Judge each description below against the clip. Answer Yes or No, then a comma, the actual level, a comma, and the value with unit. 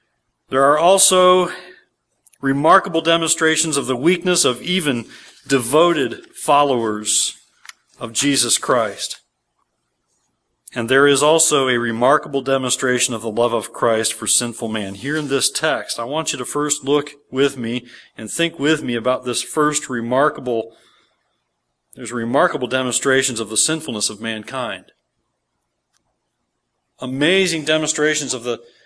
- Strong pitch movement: No, average, 4.3 semitones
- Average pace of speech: No, slow, 130 wpm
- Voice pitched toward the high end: No, low, 130 Hz